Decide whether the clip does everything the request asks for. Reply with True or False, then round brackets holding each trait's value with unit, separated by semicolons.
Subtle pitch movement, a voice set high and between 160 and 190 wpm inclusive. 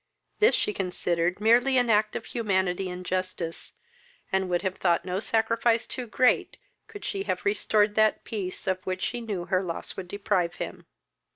False (3.9 semitones; 195 Hz; 180 wpm)